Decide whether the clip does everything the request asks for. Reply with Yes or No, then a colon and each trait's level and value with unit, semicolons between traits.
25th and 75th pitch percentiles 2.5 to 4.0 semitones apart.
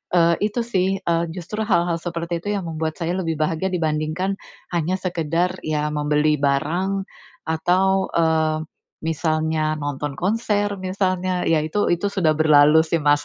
Yes: average, 3.2 semitones